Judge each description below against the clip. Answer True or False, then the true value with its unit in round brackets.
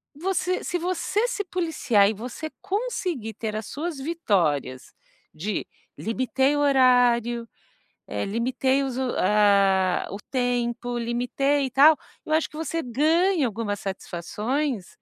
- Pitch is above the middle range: True (250 Hz)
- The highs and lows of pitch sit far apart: True (6.2 semitones)